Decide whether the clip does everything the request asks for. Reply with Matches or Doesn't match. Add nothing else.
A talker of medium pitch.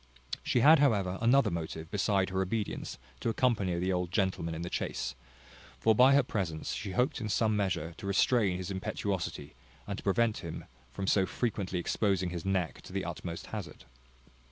Doesn't match